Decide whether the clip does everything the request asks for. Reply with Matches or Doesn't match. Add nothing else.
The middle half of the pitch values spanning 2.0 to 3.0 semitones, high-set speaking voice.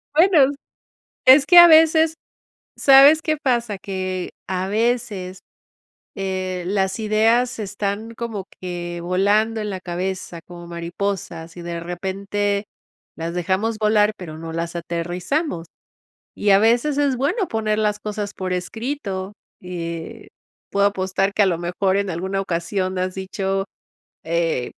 Doesn't match